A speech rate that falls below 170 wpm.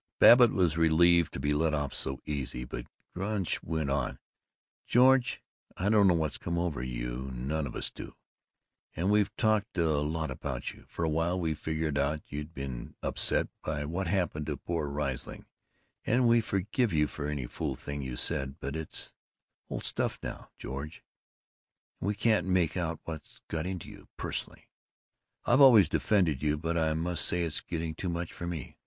No: average, 180 wpm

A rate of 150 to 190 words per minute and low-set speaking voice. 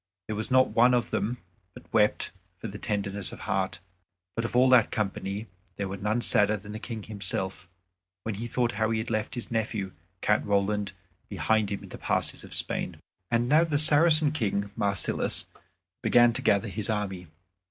Yes: average, 185 wpm; low, 110 Hz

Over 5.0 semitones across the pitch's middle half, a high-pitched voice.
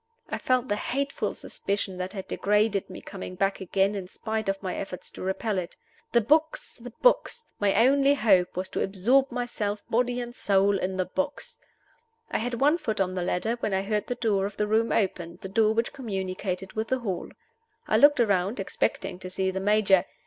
No: average, 3.9 semitones; high, 205 Hz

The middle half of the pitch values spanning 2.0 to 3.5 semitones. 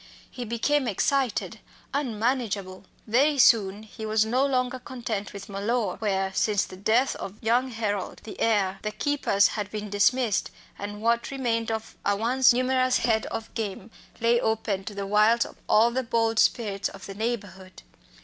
Yes: average, 3.1 semitones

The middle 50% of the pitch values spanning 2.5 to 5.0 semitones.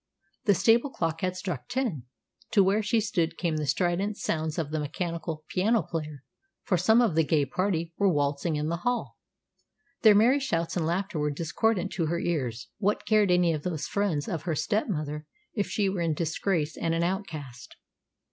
Yes: average, 4.4 semitones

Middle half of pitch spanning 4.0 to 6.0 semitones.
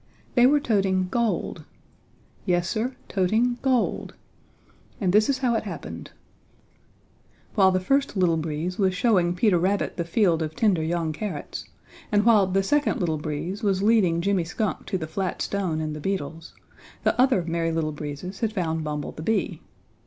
Yes: average, 4.6 semitones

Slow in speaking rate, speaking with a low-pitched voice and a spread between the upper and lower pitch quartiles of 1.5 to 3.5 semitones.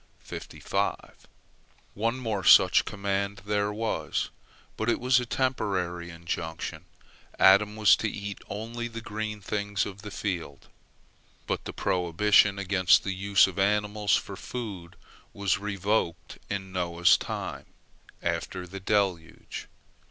Yes: slow, 120 wpm; low, 100 Hz; narrow, 2.4 semitones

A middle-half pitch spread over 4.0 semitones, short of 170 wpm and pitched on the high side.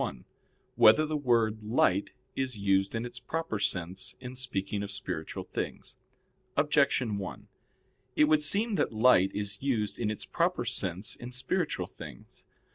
No: average, 5.0 semitones; average, 150 wpm; low, 115 Hz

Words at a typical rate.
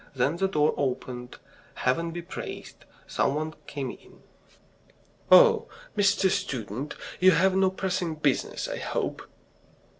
No: slow, 125 wpm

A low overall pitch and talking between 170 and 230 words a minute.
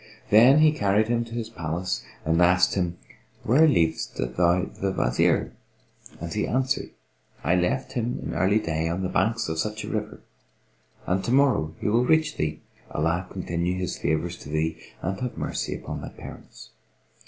Yes: very low, 95 Hz; average, 175 wpm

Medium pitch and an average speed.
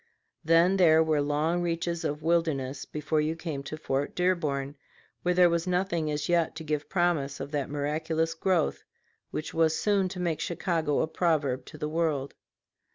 Yes: medium, 160 Hz; average, 170 wpm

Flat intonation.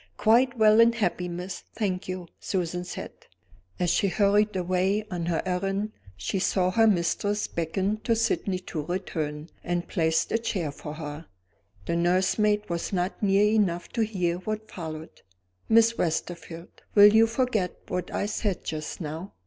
No: average, 3.7 semitones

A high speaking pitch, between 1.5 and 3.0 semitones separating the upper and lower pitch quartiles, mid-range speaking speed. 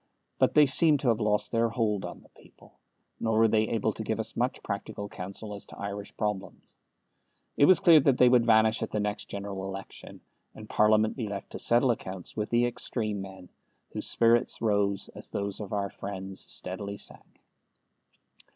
No: low, 105 Hz; narrow, 2.6 semitones; average, 190 wpm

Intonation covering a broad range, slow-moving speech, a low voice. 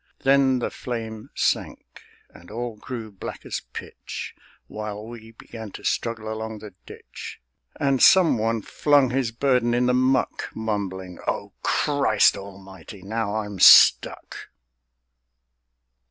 No: average, 3.2 semitones; slow, 125 wpm; low, 110 Hz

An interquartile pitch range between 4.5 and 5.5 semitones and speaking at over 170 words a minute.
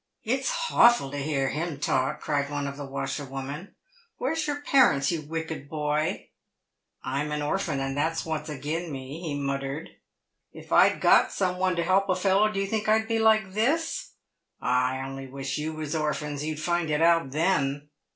Yes: average, 5.2 semitones; average, 200 wpm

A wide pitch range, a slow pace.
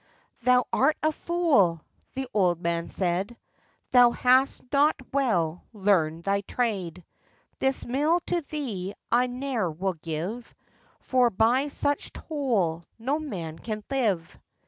Yes: wide, 6.9 semitones; slow, 125 wpm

